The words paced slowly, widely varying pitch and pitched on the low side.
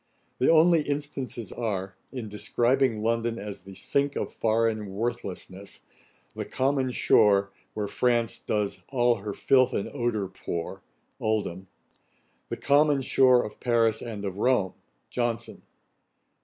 No: slow, 130 wpm; average, 4.1 semitones; low, 115 Hz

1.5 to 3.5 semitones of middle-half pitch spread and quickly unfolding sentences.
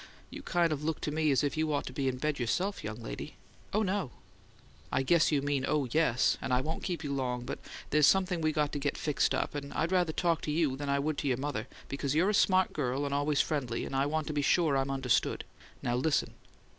Yes: average, 2.8 semitones; fast, 250 wpm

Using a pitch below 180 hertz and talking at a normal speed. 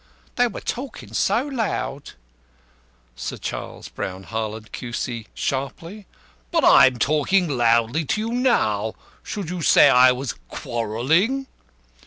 No: medium, 140 Hz; slow, 120 wpm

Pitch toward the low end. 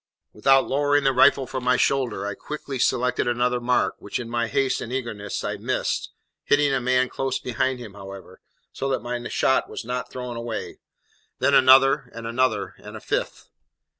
Yes: low, 125 Hz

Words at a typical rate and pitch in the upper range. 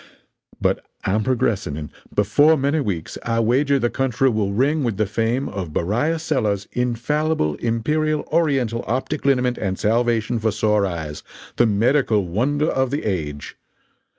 No: average, 150 wpm; low, 115 Hz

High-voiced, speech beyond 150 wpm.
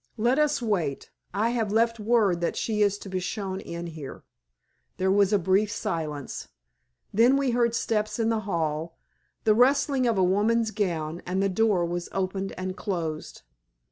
Yes: high, 200 Hz; average, 175 wpm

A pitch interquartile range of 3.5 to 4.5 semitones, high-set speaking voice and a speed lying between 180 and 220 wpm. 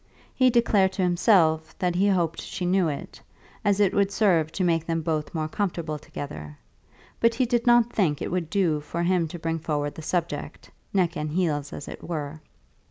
No: average, 3.9 semitones; medium, 175 Hz; average, 200 wpm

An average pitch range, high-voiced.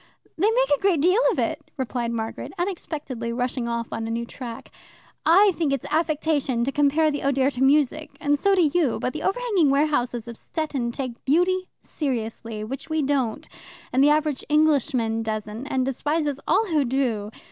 Yes: average, 4.7 semitones; very high, 275 Hz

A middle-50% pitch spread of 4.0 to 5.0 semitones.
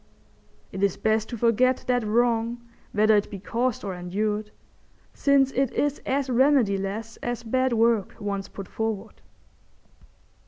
No: average, 3.1 semitones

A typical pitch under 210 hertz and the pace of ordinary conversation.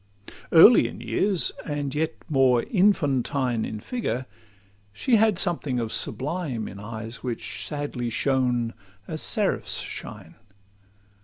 No: low, 135 Hz; slow, 120 wpm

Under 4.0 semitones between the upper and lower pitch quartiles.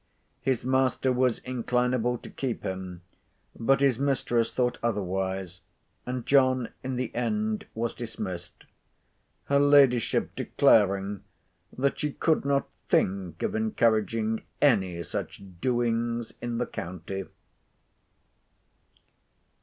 No: average, 4.5 semitones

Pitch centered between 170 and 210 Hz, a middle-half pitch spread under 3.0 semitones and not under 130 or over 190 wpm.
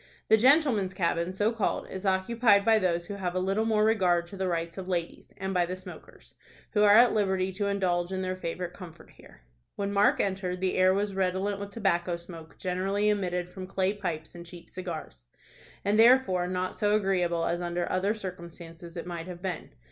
No: medium, 185 Hz; narrow, 2.5 semitones; average, 200 wpm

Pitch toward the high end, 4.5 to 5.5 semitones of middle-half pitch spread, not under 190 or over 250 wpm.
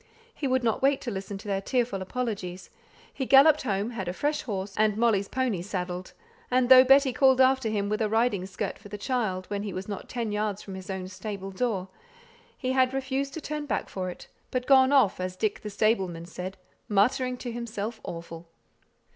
Yes: high, 215 Hz; average, 5.0 semitones; average, 200 wpm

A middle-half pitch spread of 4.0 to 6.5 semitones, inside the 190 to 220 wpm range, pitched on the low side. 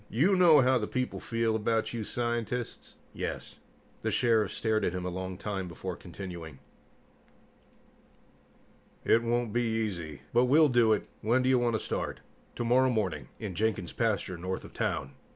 No: average, 4.4 semitones; average, 165 wpm; low, 110 Hz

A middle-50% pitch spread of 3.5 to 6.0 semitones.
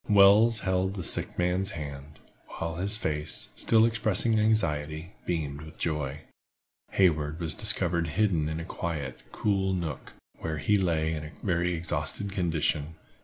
Yes: average, 4.2 semitones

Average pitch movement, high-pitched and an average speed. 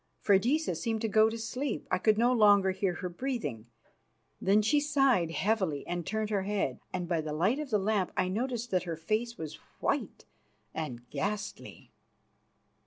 Yes: average, 4.5 semitones; high, 205 Hz; average, 175 wpm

